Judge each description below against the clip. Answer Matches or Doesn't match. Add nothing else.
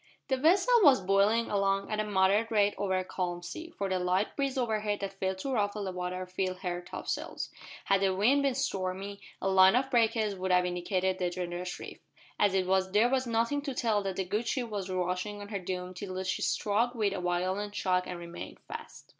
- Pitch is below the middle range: Doesn't match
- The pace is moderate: Doesn't match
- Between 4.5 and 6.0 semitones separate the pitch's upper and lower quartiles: Doesn't match